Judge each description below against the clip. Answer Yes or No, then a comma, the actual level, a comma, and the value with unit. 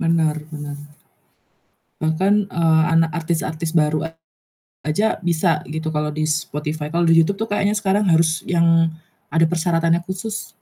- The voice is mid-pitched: Yes, medium, 165 Hz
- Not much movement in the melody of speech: Yes, narrow, 1.9 semitones